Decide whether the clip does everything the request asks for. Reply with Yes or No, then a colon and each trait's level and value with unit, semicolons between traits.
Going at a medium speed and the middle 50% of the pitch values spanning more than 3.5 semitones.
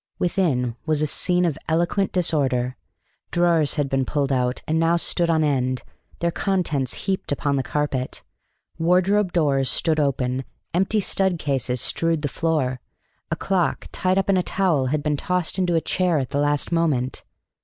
Yes: average, 170 wpm; average, 4.5 semitones